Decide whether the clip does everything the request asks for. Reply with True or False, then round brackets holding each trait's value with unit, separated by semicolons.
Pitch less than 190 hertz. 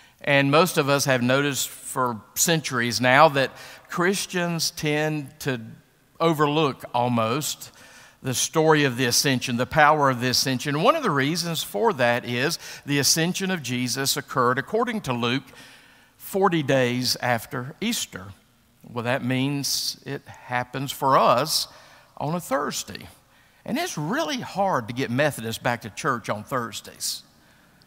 True (140 Hz)